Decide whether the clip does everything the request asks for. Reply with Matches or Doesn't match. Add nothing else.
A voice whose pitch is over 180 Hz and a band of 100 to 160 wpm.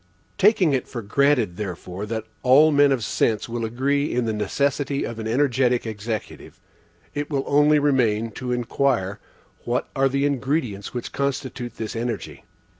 Doesn't match